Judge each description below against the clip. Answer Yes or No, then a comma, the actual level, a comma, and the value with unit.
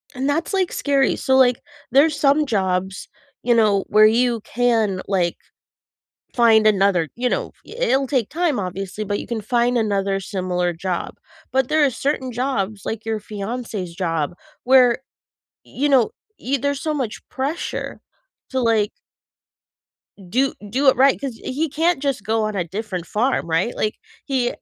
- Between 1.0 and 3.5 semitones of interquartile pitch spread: No, average, 5.1 semitones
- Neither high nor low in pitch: No, high, 235 Hz